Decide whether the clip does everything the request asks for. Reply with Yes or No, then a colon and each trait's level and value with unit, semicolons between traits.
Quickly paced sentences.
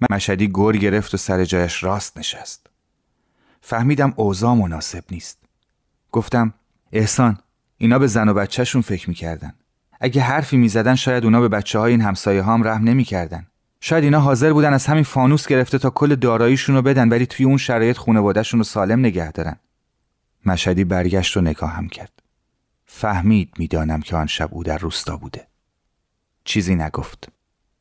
Yes: fast, 160 wpm